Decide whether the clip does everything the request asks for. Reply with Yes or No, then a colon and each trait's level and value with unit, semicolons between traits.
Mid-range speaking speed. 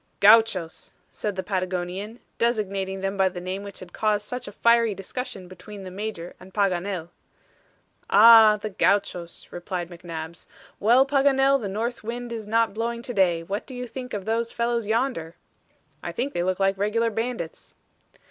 Yes: average, 165 wpm